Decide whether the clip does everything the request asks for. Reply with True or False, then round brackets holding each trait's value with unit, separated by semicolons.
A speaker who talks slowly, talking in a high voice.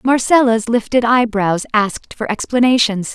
True (115 wpm; 230 Hz)